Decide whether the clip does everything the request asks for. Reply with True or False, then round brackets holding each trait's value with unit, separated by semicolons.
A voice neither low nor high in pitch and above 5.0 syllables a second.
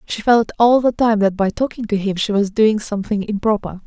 False (215 Hz; 5.5 syllables/s)